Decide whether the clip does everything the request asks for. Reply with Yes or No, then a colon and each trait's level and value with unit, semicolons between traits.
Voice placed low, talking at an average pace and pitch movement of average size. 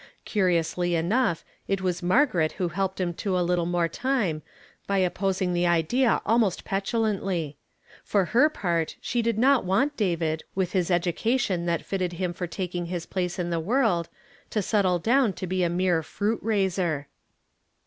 No: medium, 185 Hz; average, 165 wpm; average, 3.2 semitones